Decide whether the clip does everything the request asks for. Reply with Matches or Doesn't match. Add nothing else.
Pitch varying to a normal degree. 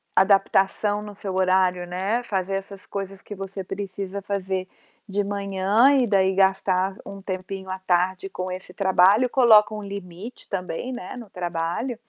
Doesn't match